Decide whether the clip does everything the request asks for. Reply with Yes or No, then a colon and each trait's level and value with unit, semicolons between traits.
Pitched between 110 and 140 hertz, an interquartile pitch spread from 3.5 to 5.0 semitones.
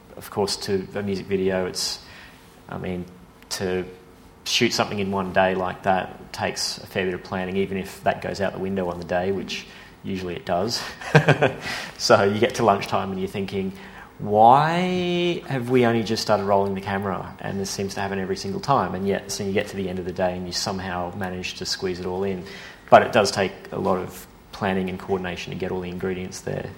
No: very low, 95 Hz; average, 4.0 semitones